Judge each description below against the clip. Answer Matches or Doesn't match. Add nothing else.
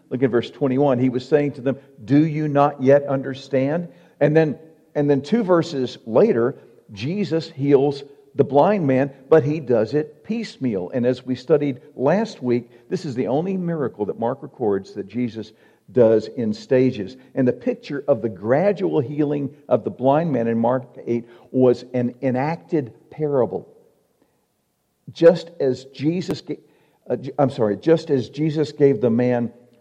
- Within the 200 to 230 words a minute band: Doesn't match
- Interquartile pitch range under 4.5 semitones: Matches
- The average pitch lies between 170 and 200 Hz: Doesn't match